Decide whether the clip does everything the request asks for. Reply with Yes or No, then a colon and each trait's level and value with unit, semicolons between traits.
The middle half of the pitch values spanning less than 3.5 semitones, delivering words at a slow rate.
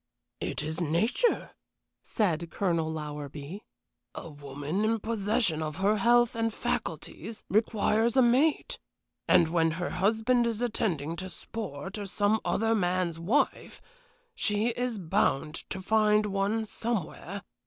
No: average, 5.2 semitones; slow, 130 wpm